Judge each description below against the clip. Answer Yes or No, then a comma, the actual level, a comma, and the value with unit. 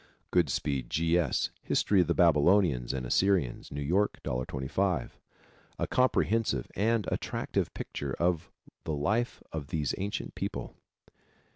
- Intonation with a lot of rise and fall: Yes, wide, 6.2 semitones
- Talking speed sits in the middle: No, slow, 125 wpm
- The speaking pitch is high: No, very low, 85 Hz